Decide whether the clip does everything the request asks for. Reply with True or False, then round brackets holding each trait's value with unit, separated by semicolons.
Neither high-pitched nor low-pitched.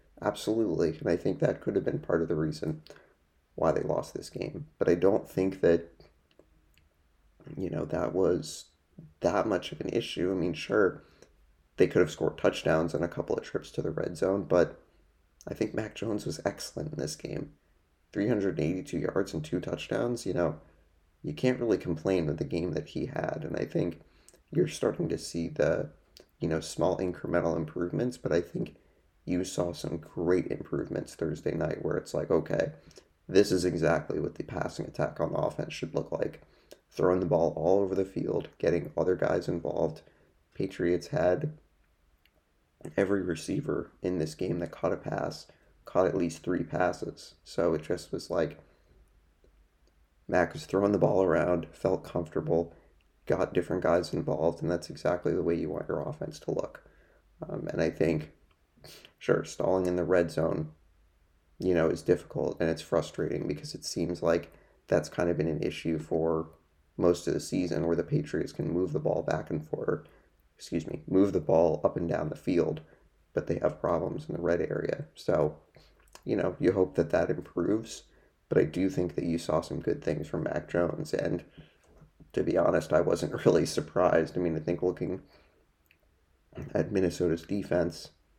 False (85 Hz)